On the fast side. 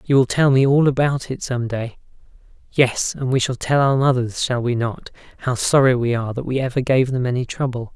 Yes: fast, 210 wpm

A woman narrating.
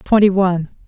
Yes: female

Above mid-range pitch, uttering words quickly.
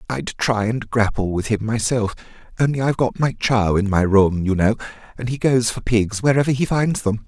No: low, 115 Hz; fast, 215 wpm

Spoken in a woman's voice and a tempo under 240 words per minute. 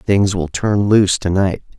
No: male; average, 200 wpm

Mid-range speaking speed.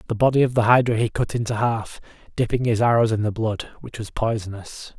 No: fast, 215 wpm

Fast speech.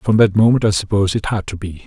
Yes: fast, 290 wpm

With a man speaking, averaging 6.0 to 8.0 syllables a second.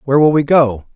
Yes: male; 6.3 syllables/s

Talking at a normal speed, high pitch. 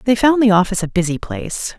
No: fast, 235 wpm; high, 205 Hz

